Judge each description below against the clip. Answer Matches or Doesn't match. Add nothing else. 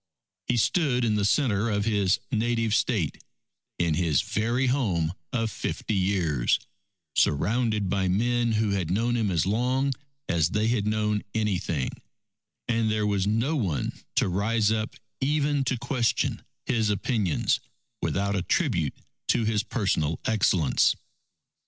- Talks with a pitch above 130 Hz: Doesn't match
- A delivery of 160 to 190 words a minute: Doesn't match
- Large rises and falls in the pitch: Doesn't match